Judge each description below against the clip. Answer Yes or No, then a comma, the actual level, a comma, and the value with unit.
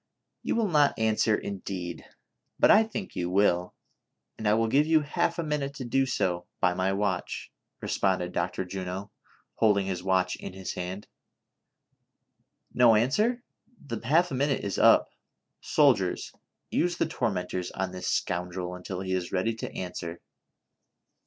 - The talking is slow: No, average, 160 wpm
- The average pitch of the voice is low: Yes, low, 100 Hz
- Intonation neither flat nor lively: No, wide, 6.9 semitones